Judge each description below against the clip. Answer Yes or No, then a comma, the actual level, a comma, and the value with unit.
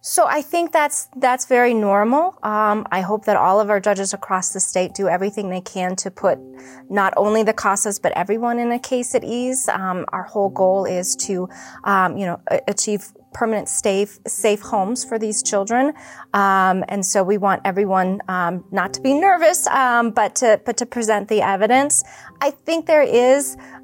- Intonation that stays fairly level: No, average, 4.1 semitones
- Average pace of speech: Yes, average, 190 wpm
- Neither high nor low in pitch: No, high, 210 Hz